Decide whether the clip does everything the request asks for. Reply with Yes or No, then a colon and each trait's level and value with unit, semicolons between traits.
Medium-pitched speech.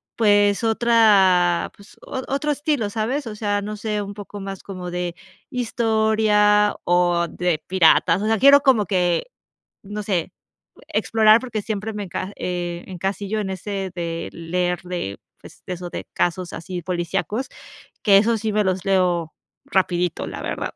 No: high, 200 Hz